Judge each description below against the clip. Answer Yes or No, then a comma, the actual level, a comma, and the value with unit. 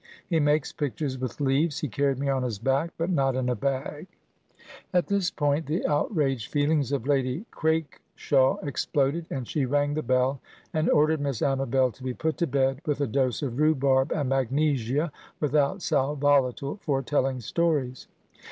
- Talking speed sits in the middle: Yes, average, 170 wpm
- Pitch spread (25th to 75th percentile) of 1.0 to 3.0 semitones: Yes, narrow, 2.4 semitones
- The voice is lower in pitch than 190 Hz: Yes, medium, 140 Hz